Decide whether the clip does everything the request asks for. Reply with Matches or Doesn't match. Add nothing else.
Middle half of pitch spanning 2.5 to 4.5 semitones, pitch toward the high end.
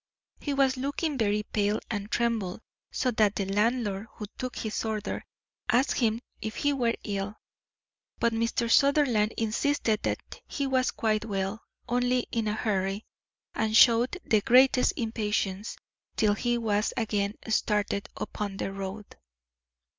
Matches